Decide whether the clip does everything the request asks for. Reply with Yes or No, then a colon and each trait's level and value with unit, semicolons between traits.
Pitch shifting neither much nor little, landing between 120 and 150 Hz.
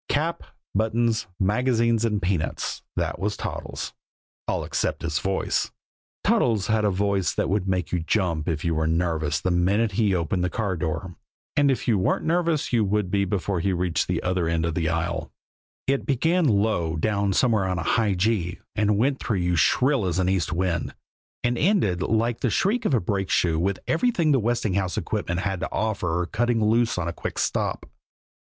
No: average, 4.7 semitones; low, 100 Hz